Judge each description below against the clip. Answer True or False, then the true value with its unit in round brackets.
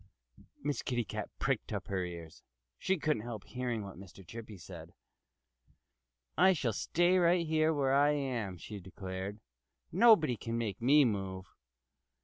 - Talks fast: False (140 wpm)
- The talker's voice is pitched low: True (115 Hz)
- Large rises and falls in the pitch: True (7.3 semitones)